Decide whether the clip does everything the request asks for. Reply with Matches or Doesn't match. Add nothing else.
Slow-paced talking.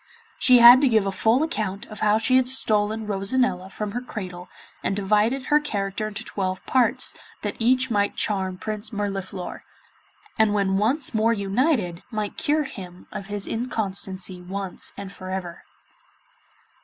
Doesn't match